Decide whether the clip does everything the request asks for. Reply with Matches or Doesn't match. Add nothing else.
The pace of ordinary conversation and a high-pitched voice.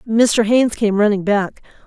Matches